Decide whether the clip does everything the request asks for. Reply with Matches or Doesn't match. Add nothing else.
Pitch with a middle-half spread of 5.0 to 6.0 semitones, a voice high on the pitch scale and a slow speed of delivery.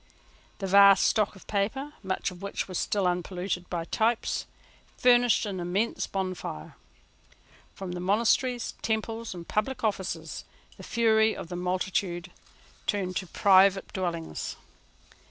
Doesn't match